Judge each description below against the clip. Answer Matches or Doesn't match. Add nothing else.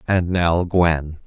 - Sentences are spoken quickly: Doesn't match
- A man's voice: Matches